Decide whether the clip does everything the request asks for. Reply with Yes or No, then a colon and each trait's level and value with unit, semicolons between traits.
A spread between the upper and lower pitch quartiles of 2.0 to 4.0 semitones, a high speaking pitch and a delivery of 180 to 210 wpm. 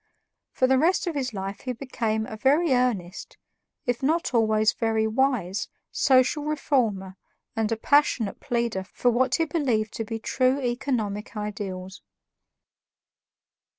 No: average, 3.7 semitones; high, 235 Hz; slow, 135 wpm